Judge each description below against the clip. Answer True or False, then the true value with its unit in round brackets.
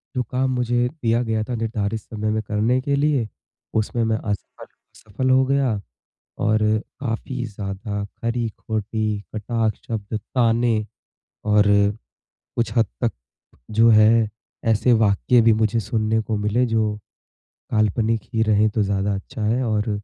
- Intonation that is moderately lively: False (1.9 semitones)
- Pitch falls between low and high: False (110 Hz)